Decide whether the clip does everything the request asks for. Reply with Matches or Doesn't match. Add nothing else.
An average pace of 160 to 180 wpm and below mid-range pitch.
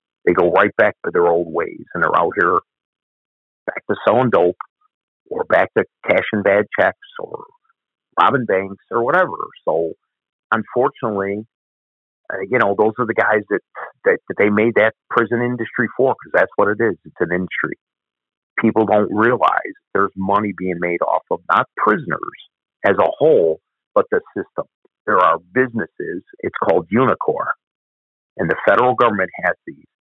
Matches